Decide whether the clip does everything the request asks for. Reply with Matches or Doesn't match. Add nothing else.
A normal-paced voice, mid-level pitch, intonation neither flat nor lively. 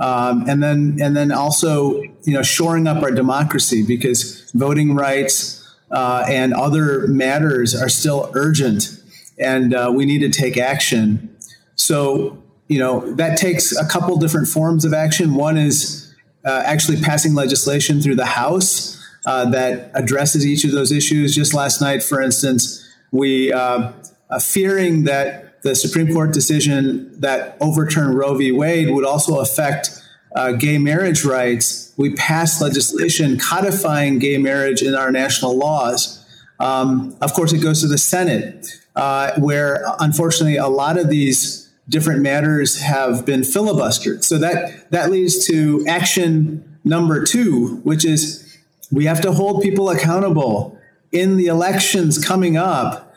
Matches